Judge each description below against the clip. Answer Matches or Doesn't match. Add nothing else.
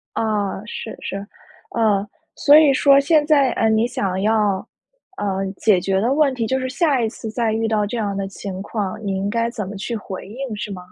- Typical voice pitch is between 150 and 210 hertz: Doesn't match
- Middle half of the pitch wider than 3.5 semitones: Matches